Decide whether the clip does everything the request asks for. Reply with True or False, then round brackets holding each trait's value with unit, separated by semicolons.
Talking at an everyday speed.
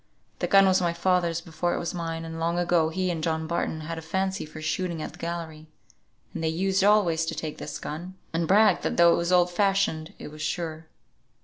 False (225 wpm)